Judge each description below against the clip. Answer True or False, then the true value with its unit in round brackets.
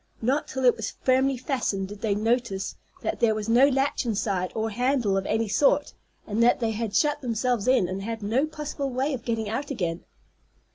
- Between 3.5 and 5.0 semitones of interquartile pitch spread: True (4.0 semitones)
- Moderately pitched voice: False (230 Hz)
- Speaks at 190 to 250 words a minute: True (200 wpm)